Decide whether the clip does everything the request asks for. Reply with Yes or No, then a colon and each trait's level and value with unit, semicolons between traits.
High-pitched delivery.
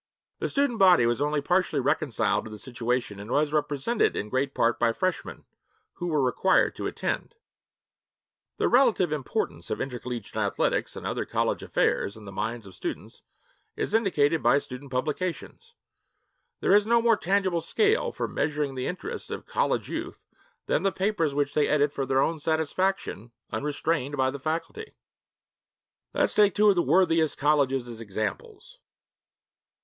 No: medium, 150 Hz